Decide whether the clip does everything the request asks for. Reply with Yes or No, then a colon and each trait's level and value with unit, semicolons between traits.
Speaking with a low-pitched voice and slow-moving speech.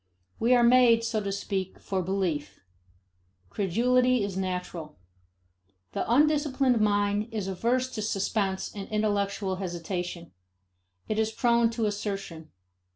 No: high, 205 Hz; slow, 120 wpm